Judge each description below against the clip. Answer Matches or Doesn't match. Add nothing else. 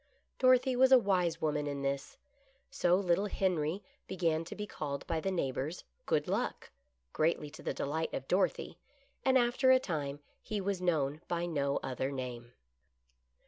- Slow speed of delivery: Doesn't match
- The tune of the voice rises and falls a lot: Matches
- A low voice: Doesn't match